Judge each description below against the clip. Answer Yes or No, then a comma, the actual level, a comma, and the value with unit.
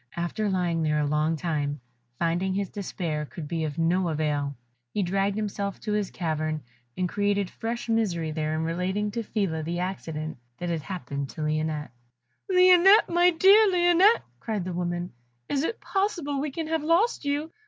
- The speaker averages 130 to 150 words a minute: No, average, 175 wpm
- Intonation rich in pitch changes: Yes, wide, 7.0 semitones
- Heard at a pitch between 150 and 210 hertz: Yes, medium, 185 Hz